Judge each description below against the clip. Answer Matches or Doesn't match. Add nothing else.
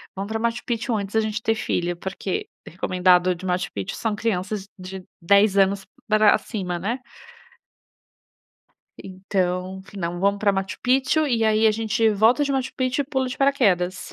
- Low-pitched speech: Doesn't match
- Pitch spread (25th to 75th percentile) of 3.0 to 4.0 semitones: Matches